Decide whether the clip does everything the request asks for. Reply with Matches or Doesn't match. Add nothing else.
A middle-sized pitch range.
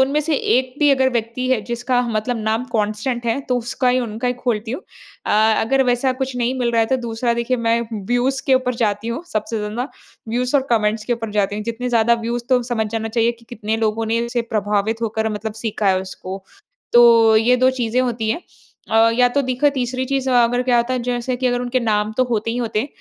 Doesn't match